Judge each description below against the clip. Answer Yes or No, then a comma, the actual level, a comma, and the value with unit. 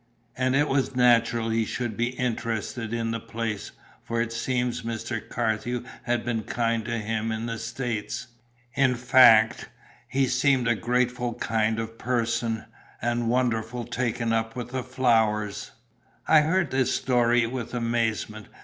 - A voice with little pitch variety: Yes, narrow, 1.7 semitones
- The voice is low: Yes, low, 120 Hz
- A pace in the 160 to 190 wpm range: No, average, 145 wpm